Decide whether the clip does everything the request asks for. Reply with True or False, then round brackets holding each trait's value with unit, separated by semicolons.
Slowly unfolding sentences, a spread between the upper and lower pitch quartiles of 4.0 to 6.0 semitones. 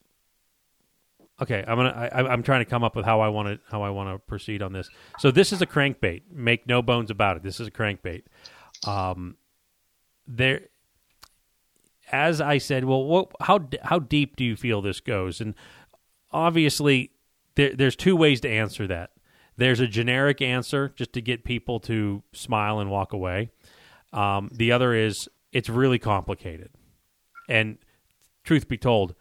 False (170 wpm; 4.6 semitones)